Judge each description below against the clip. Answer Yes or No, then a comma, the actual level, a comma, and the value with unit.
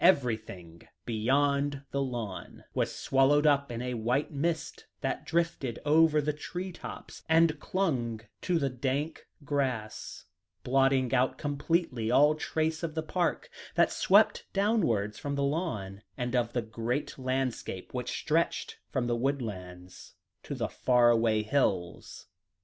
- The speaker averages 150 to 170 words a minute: No, average, 140 wpm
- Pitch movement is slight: No, average, 4.6 semitones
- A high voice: No, low, 135 Hz